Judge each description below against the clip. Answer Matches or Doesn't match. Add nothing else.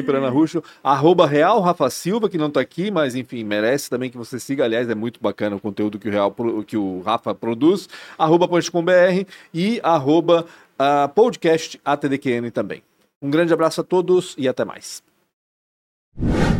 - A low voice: Doesn't match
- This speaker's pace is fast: Doesn't match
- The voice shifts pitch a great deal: Matches